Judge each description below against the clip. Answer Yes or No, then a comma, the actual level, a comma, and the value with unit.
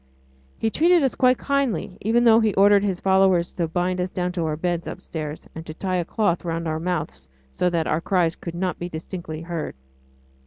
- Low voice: No, medium, 180 Hz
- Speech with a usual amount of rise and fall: Yes, average, 3.3 semitones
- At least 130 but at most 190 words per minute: No, fast, 205 wpm